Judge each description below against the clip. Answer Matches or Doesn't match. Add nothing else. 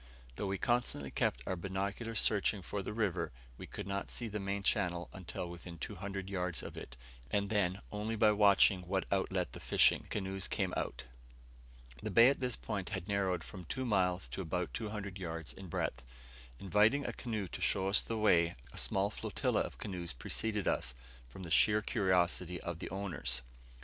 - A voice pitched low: Matches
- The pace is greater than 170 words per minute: Matches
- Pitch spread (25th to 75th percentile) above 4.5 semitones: Doesn't match